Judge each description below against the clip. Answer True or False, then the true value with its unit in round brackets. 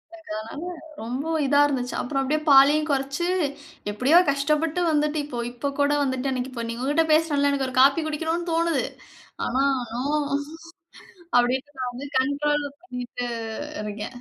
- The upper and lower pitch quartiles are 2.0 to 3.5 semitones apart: True (3.1 semitones)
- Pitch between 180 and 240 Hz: False (280 Hz)